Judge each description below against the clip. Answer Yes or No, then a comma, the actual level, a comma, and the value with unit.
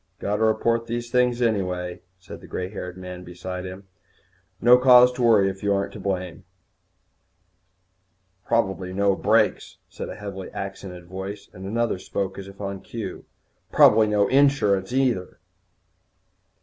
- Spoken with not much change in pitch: No, average, 3.7 semitones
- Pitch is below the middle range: Yes, low, 100 Hz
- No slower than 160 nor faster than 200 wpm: No, average, 150 wpm